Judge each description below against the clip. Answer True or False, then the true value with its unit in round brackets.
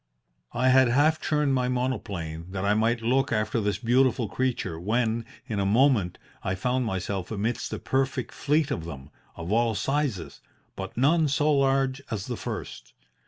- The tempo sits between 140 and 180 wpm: True (165 wpm)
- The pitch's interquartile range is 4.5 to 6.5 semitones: True (4.9 semitones)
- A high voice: False (120 Hz)